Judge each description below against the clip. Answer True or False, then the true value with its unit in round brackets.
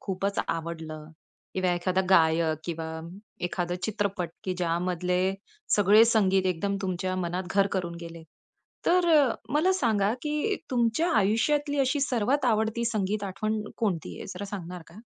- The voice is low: False (195 Hz)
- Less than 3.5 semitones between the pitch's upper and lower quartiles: False (4.1 semitones)